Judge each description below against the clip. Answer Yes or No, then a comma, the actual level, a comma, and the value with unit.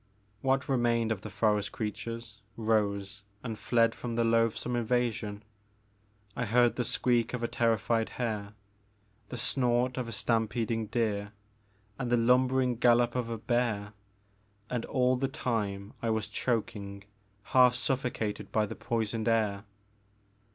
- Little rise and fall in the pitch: Yes, narrow, 2.2 semitones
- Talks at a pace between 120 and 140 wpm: Yes, slow, 135 wpm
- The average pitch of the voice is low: Yes, low, 115 Hz